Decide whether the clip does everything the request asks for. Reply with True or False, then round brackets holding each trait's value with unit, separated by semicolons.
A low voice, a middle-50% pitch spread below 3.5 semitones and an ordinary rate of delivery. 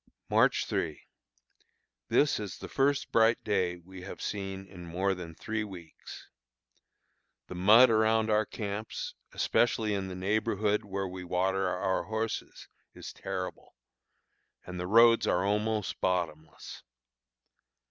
False (100 Hz; 3.1 semitones; 125 wpm)